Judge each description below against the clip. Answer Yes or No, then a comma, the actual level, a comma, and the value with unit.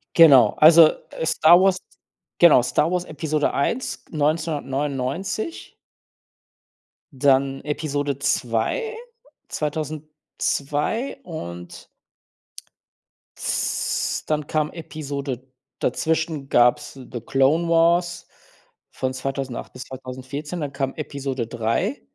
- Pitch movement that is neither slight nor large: Yes, average, 3.3 semitones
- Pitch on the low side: No, medium, 145 Hz